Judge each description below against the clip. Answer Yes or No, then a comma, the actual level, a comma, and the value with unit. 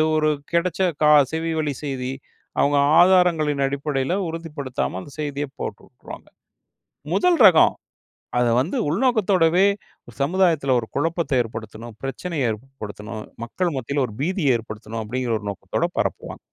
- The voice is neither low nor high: Yes, medium, 145 Hz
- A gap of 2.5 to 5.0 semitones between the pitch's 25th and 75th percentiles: No, wide, 5.5 semitones